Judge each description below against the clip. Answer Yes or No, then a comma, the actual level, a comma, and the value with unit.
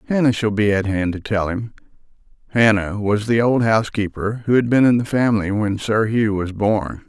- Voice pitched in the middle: No, low, 110 Hz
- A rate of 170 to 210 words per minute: Yes, fast, 205 wpm